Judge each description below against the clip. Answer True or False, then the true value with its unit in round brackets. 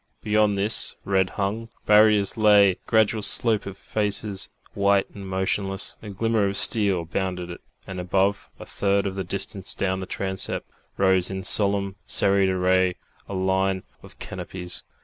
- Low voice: True (100 Hz)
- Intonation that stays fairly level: True (1.4 semitones)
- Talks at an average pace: True (155 wpm)